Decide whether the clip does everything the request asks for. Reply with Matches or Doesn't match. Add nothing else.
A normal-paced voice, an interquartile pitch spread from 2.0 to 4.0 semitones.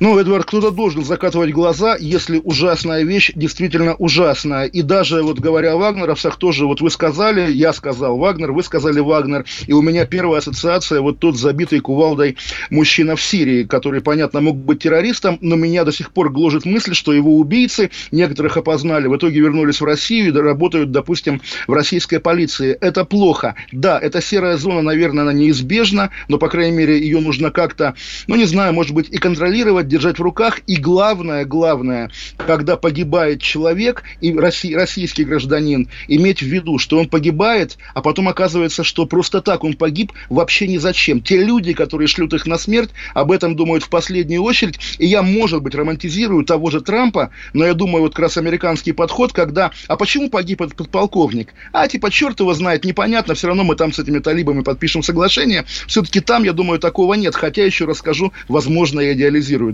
Doesn't match